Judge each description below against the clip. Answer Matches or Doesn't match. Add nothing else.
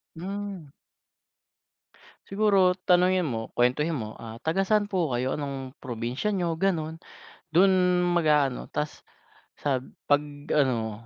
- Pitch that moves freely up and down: Matches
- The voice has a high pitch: Doesn't match